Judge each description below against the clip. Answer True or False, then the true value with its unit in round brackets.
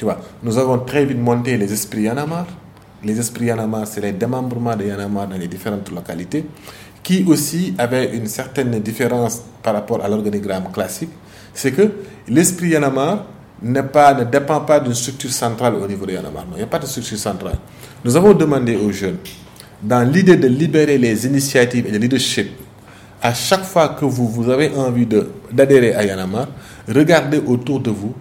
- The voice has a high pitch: False (120 Hz)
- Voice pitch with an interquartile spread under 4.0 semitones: False (4.6 semitones)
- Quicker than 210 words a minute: False (185 wpm)